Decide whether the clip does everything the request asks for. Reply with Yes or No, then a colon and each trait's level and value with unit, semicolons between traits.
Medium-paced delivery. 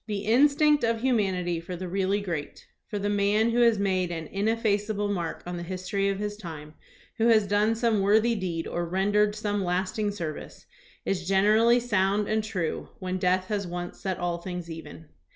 Yes: average, 190 wpm